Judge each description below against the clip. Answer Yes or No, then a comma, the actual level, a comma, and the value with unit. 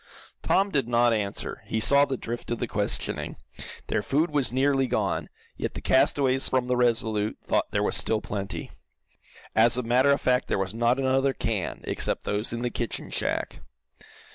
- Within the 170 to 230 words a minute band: Yes, average, 180 wpm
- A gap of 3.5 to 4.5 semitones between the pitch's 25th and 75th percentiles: No, average, 3.0 semitones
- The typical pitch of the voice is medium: No, low, 120 Hz